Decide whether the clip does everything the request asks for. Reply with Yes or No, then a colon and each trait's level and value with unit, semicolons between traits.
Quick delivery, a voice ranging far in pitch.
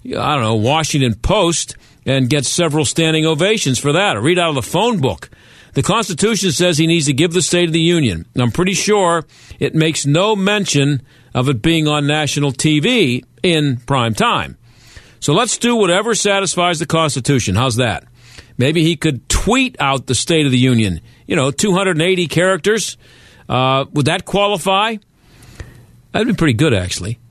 No: average, 175 wpm; wide, 5.7 semitones